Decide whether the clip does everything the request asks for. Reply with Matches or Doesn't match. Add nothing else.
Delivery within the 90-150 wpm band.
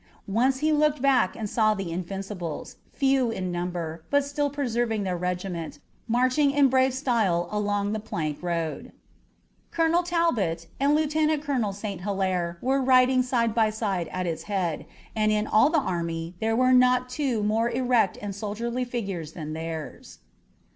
Doesn't match